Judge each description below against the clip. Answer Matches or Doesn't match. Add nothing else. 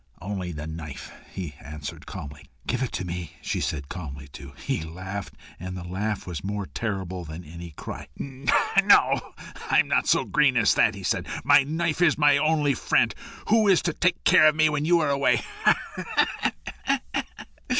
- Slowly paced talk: Doesn't match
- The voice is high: Doesn't match